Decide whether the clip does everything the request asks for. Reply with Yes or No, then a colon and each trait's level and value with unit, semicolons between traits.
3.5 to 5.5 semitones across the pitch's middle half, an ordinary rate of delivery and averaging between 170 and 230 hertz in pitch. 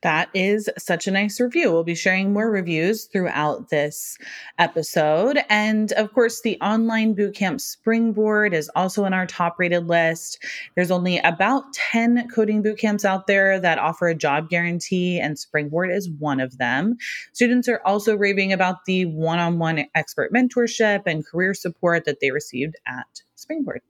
Yes: average, 4.3 semitones; average, 165 wpm; medium, 185 Hz